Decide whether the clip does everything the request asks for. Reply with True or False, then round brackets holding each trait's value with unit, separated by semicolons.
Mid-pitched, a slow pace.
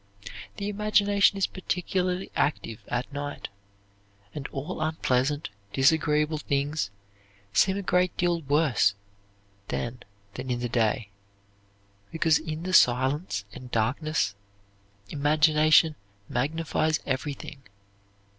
True (150 Hz; 100 wpm)